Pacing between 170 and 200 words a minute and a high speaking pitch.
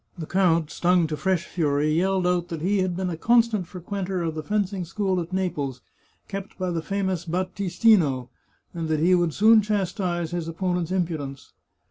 No: average, 180 wpm; medium, 180 Hz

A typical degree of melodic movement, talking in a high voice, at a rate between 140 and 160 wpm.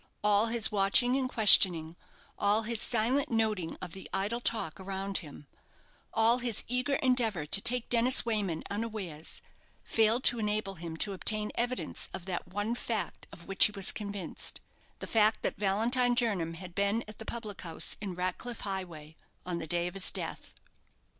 No: average, 3.8 semitones; high, 210 Hz; average, 170 wpm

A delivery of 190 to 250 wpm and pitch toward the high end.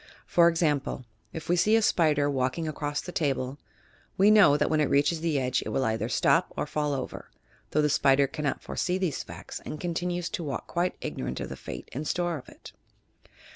No: fast, 205 wpm; medium, 150 Hz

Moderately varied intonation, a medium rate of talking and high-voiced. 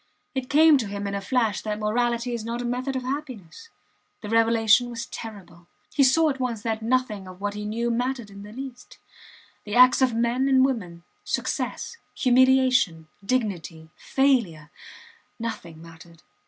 Yes: average, 4.0 semitones; average, 165 wpm; high, 230 Hz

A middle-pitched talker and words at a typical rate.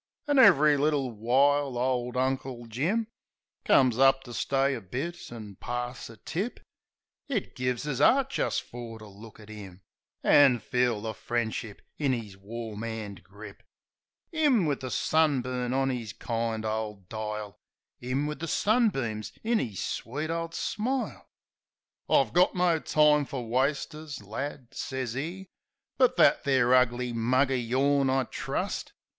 No: low, 130 Hz; average, 150 wpm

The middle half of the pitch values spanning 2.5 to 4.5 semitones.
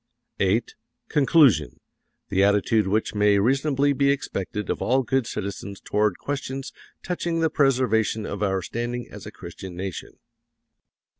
No: average, 5.3 semitones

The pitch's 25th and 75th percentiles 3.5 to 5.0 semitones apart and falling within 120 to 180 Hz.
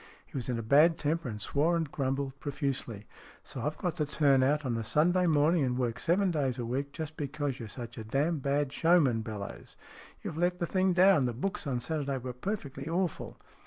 Yes: average, 4.5 semitones; medium, 140 Hz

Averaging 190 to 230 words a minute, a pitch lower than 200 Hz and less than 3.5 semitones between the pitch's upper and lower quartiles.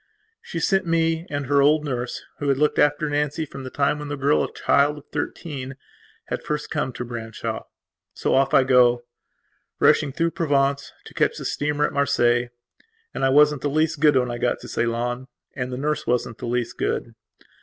Yes: average, 195 wpm; medium, 140 Hz; average, 2.9 semitones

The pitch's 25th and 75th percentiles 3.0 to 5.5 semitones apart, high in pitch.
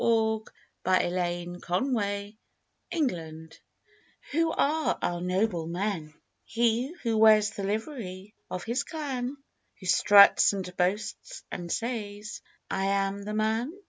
Yes: average, 3.9 semitones; high, 205 Hz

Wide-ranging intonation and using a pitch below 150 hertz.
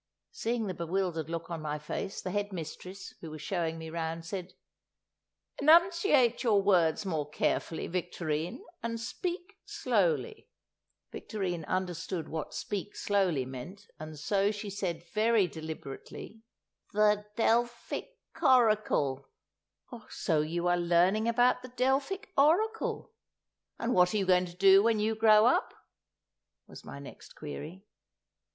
No: wide, 5.8 semitones; high, 195 Hz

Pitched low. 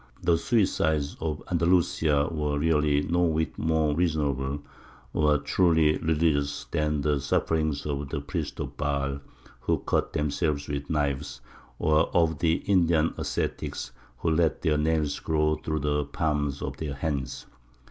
Yes: very low, 75 Hz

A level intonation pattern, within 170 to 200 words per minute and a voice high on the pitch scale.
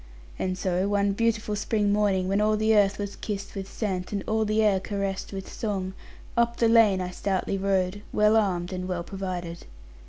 Yes: narrow, 2.1 semitones; average, 190 wpm; high, 200 Hz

